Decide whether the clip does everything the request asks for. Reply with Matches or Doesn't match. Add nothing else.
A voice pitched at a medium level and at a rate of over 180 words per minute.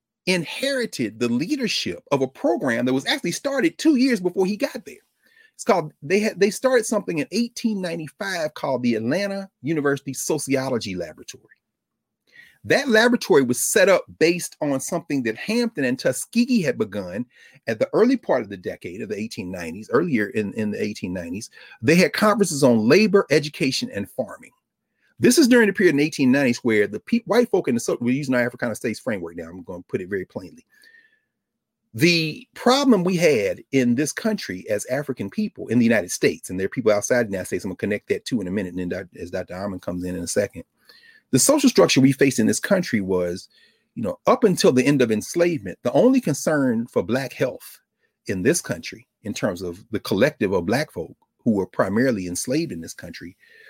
Matches